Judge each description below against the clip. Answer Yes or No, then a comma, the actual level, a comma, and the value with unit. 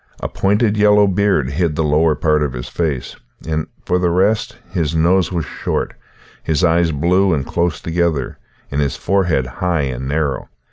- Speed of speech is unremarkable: Yes, average, 175 wpm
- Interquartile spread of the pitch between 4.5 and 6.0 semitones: No, average, 3.6 semitones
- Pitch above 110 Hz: No, very low, 80 Hz